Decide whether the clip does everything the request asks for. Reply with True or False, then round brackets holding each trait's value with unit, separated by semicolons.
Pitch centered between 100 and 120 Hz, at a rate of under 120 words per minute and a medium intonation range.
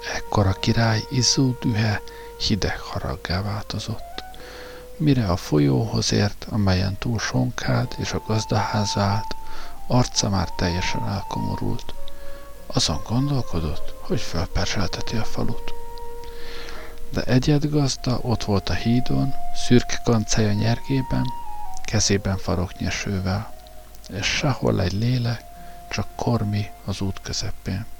True (110 Hz; 105 wpm; 4.8 semitones)